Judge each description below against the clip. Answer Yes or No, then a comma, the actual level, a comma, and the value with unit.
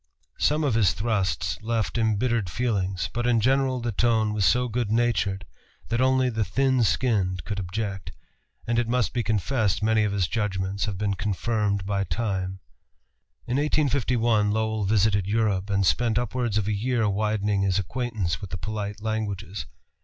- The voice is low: Yes, low, 110 Hz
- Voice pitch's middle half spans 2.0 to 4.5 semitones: Yes, average, 3.1 semitones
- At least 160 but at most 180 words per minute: Yes, average, 165 wpm